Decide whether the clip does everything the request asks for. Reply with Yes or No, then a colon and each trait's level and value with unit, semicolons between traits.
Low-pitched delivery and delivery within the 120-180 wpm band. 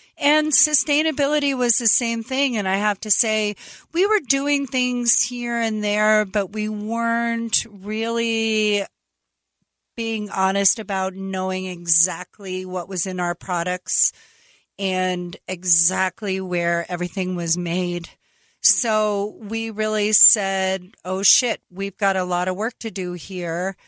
No: high, 205 Hz; slow, 135 wpm